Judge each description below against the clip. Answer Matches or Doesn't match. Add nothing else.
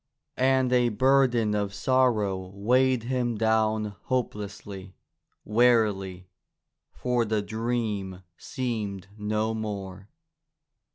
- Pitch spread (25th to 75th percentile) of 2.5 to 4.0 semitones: Matches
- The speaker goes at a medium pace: Doesn't match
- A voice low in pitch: Matches